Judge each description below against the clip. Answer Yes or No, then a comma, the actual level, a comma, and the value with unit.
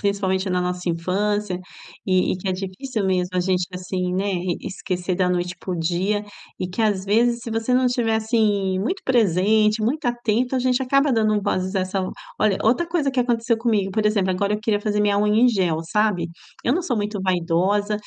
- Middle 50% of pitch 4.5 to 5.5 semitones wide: No, average, 3.4 semitones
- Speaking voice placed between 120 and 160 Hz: No, high, 205 Hz